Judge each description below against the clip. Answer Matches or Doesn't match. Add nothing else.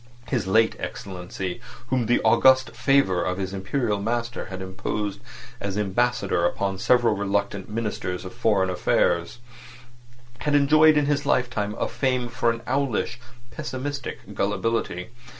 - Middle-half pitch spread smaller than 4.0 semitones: Doesn't match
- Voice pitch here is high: Doesn't match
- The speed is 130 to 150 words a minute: Matches